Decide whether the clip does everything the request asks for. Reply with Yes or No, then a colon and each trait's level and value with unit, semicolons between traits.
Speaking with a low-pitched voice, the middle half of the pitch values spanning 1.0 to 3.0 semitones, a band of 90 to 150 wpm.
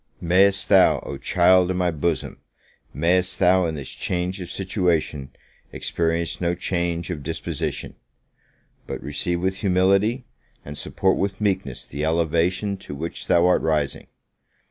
Yes: very low, 90 Hz; narrow, 2.4 semitones; average, 140 wpm